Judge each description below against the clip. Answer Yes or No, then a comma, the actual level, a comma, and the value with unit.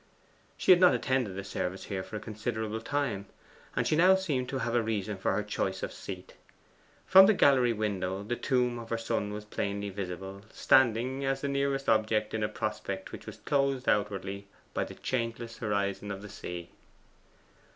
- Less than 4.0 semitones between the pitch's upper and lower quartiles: No, average, 4.5 semitones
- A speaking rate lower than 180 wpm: No, average, 185 wpm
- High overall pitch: No, low, 110 Hz